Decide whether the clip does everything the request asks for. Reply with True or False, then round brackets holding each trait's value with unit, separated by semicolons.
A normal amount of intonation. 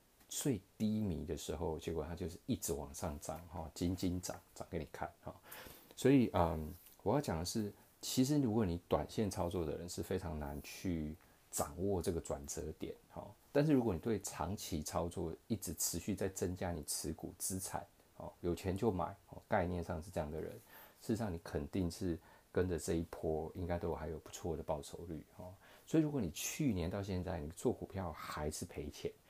True (3.5 semitones)